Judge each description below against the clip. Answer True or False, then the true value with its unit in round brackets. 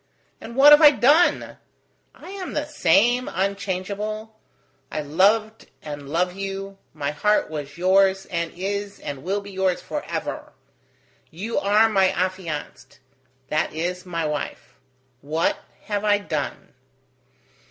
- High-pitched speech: True (195 Hz)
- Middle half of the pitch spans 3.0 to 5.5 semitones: True (4.0 semitones)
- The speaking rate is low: True (130 wpm)